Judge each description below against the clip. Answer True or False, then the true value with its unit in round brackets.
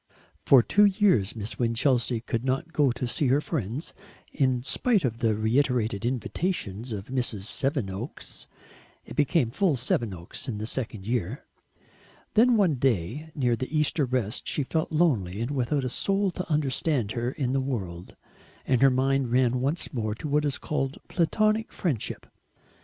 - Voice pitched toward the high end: False (130 Hz)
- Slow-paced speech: False (160 wpm)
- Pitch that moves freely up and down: False (4.5 semitones)